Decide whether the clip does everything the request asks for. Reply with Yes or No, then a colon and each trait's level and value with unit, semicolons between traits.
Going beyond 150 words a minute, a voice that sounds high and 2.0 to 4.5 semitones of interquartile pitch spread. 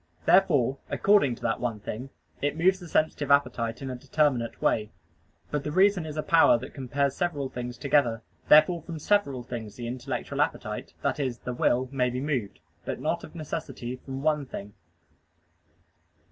No: average, 175 wpm; low, 135 Hz; average, 4.0 semitones